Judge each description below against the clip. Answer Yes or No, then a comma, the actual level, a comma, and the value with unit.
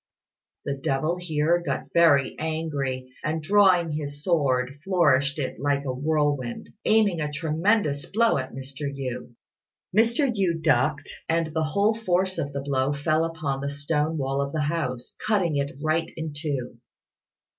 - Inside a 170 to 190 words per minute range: No, average, 155 wpm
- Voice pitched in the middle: Yes, medium, 150 Hz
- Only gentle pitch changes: No, average, 3.2 semitones